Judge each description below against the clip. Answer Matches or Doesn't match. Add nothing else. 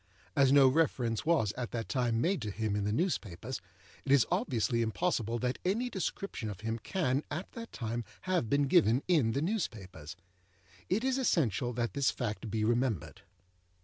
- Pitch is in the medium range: Doesn't match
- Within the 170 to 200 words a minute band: Matches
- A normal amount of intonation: Doesn't match